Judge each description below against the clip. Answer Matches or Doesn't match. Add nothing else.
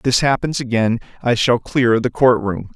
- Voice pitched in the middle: Doesn't match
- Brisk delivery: Doesn't match